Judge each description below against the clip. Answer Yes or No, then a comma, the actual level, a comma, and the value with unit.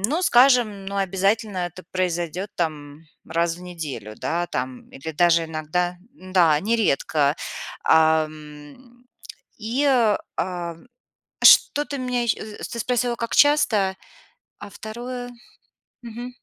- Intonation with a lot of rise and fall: Yes, wide, 6.5 semitones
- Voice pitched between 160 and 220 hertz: Yes, medium, 185 Hz